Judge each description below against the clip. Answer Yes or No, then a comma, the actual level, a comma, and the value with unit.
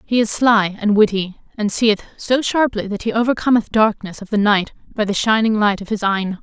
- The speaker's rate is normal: No, fast, 215 wpm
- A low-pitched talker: No, high, 215 Hz